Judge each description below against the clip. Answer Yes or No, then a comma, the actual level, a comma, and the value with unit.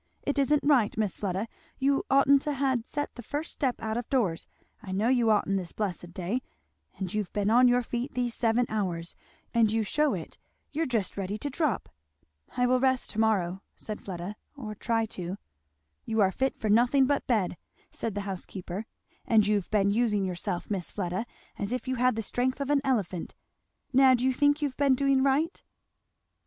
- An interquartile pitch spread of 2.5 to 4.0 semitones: No, average, 4.7 semitones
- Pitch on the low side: No, high, 225 Hz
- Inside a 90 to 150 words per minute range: No, average, 195 wpm